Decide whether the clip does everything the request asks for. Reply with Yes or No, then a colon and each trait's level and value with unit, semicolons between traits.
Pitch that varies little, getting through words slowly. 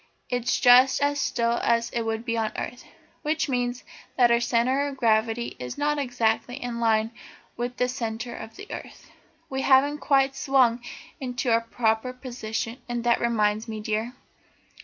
No: narrow, 2.3 semitones; average, 165 wpm